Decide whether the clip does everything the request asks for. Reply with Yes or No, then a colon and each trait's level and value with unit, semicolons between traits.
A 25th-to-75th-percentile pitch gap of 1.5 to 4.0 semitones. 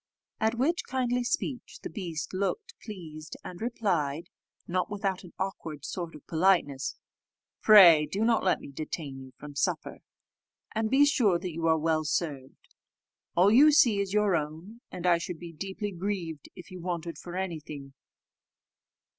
No: average, 4.9 semitones